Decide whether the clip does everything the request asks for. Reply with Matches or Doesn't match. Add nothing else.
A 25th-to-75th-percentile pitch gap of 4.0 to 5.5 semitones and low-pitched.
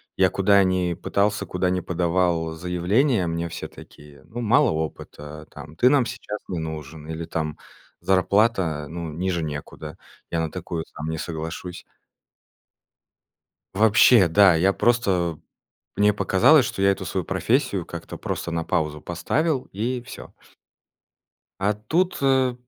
Matches